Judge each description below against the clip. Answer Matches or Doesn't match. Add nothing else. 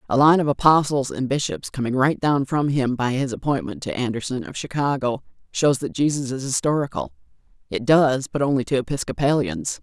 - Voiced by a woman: Matches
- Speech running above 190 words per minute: Doesn't match